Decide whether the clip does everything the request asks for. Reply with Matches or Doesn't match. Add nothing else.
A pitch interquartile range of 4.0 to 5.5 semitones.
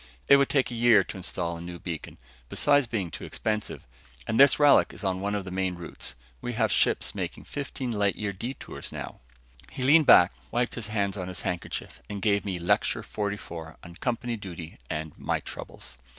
Matches